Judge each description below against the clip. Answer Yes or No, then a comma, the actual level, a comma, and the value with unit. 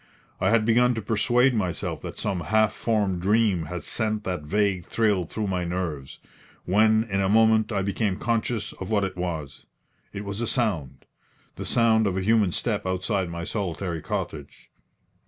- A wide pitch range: No, average, 3.5 semitones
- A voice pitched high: No, low, 100 Hz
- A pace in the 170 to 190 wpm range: Yes, average, 175 wpm